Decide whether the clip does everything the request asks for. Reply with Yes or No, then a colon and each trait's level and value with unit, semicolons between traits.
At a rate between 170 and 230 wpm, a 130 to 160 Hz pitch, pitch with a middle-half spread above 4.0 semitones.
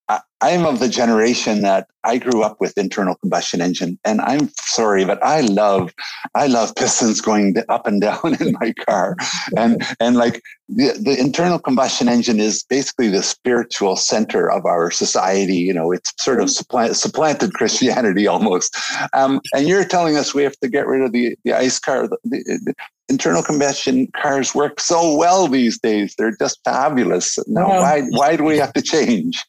Yes: average, 185 wpm; low, 135 Hz; average, 5.1 semitones